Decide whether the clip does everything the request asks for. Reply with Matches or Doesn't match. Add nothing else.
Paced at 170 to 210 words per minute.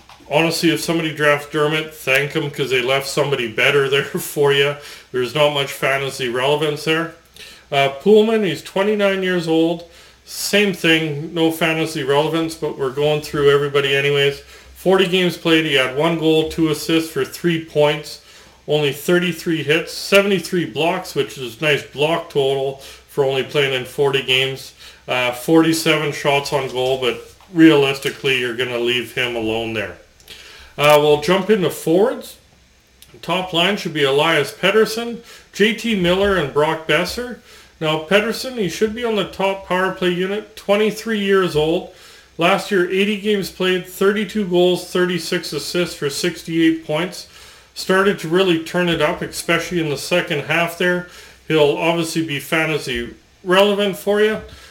Doesn't match